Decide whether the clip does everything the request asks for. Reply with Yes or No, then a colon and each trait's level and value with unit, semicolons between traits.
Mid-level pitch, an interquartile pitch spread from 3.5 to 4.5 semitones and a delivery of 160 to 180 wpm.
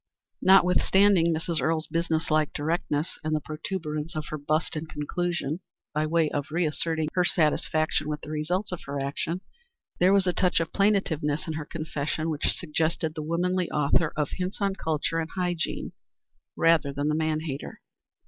No: medium, 160 Hz; narrow, 2.5 semitones; average, 165 wpm